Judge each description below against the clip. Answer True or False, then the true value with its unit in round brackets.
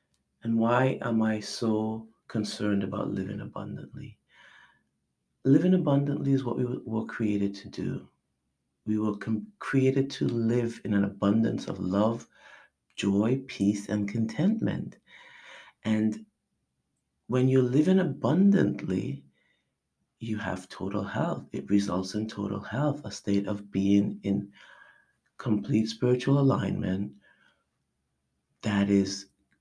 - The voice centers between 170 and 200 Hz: False (105 Hz)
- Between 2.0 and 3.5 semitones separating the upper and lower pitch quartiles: False (3.9 semitones)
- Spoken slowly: True (115 wpm)